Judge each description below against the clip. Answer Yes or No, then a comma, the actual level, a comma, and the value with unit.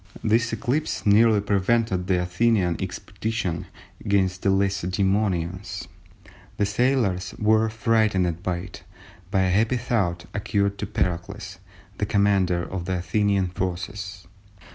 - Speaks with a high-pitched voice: No, low, 100 Hz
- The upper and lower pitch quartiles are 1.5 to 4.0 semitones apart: Yes, average, 3.0 semitones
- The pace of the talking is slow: Yes, slow, 120 wpm